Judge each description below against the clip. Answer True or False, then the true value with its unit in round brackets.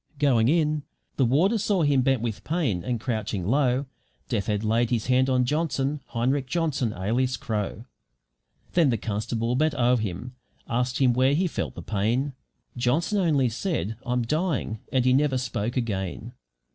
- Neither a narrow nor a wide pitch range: True (4.1 semitones)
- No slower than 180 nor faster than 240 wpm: False (165 wpm)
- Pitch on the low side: True (125 Hz)